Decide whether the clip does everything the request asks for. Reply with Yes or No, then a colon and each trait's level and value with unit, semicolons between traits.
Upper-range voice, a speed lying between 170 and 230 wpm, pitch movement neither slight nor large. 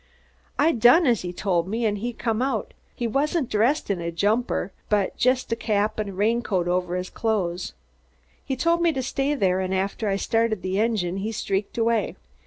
Yes: high, 215 Hz; fast, 205 wpm; average, 4.0 semitones